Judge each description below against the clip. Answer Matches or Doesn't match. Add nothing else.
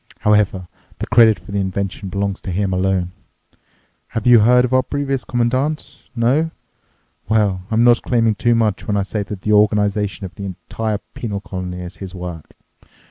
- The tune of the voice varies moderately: Matches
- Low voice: Matches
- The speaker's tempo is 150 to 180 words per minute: Matches